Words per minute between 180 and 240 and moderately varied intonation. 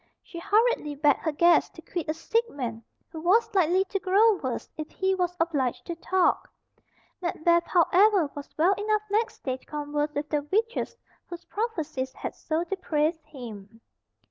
No: average, 170 wpm; average, 4.6 semitones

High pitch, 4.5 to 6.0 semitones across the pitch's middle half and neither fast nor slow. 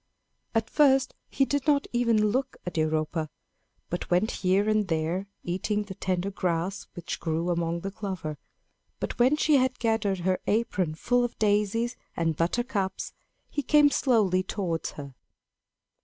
Yes: high, 200 Hz; wide, 5.4 semitones; average, 150 wpm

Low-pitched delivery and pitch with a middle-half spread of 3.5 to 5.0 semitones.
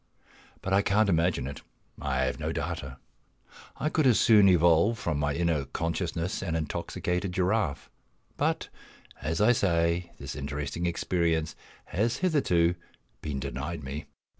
Yes: very low, 85 Hz; average, 4.7 semitones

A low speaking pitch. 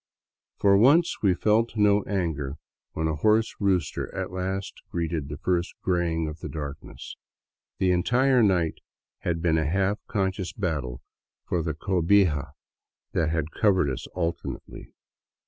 Yes: very low, 90 Hz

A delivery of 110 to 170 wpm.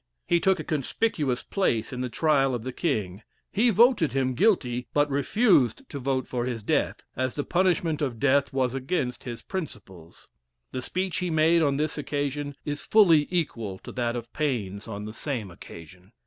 No: average, 180 wpm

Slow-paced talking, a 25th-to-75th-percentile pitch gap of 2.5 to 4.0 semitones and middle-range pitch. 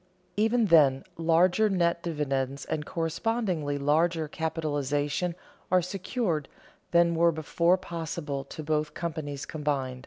Yes: slow, 115 wpm; average, 3.0 semitones; medium, 160 Hz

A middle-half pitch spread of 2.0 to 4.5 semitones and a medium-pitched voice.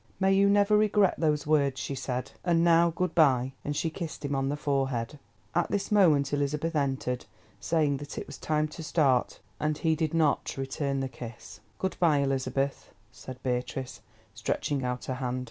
Yes: average, 3.7 semitones; medium, 145 Hz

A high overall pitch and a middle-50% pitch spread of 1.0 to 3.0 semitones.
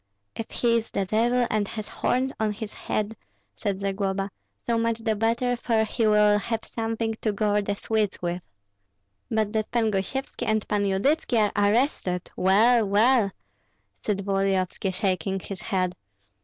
Yes: high, 210 Hz; narrow, 2.5 semitones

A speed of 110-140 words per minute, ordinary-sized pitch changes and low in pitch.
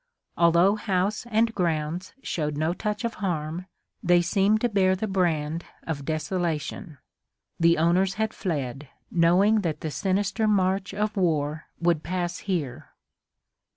No: slow, 135 wpm; average, 3.8 semitones; medium, 180 Hz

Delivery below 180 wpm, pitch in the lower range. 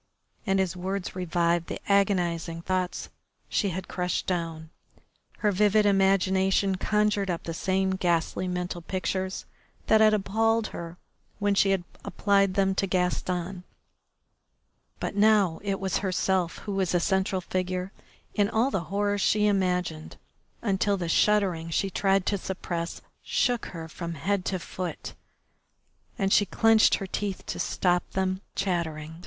No: average, 145 wpm; high, 190 Hz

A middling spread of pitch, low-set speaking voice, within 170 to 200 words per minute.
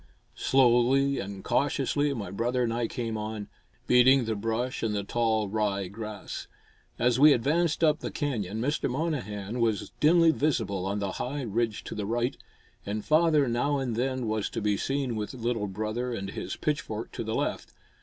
Yes: average, 4.2 semitones; low, 120 Hz; average, 175 wpm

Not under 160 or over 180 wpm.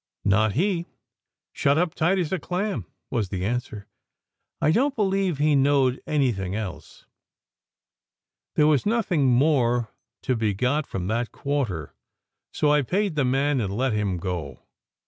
No: average, 150 wpm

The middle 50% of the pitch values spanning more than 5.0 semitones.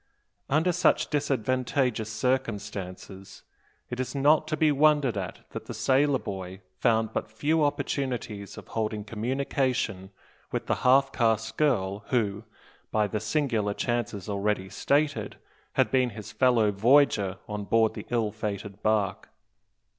No: average, 4.7 semitones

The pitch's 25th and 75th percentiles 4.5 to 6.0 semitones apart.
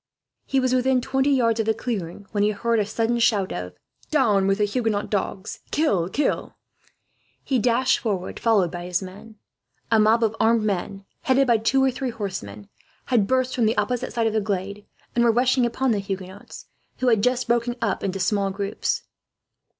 No: average, 3.7 semitones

